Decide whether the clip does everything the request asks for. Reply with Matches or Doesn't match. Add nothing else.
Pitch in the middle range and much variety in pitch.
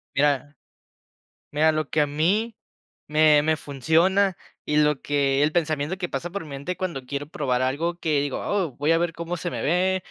Doesn't match